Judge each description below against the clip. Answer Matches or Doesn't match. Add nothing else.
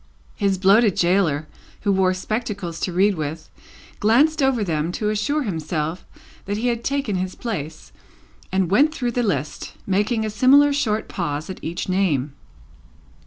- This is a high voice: Matches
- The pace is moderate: Matches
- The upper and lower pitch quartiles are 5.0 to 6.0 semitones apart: Matches